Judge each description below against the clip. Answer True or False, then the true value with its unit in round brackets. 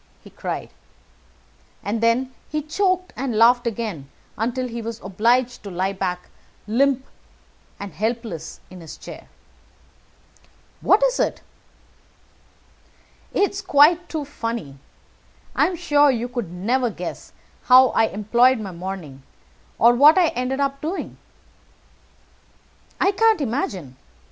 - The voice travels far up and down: True (5.9 semitones)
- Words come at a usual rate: False (125 wpm)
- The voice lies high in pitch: True (240 Hz)